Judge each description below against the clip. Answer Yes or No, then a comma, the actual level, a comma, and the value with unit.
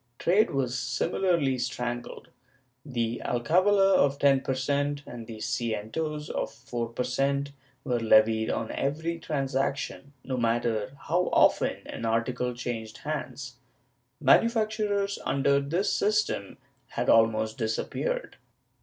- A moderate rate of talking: No, slow, 120 wpm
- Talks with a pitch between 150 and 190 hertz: No, low, 135 Hz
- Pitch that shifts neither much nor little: Yes, average, 4.6 semitones